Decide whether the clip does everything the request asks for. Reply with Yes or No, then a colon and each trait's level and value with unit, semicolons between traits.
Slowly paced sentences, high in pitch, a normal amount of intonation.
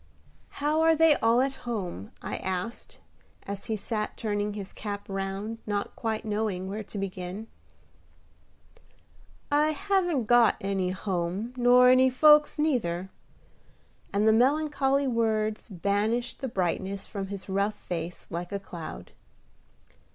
Yes: slow, 130 wpm; high, 215 Hz; average, 4.5 semitones